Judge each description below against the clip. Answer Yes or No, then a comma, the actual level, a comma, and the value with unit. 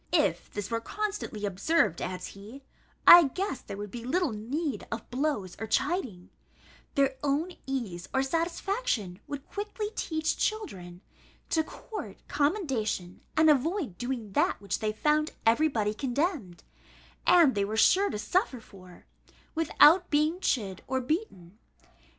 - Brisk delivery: No, average, 140 wpm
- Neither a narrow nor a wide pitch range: No, wide, 7.8 semitones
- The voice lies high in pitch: Yes, very high, 265 Hz